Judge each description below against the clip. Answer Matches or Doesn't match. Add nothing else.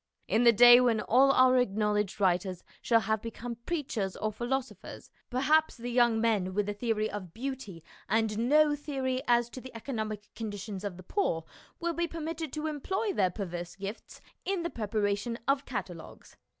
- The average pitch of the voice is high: Matches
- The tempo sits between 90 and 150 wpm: Doesn't match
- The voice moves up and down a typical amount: Matches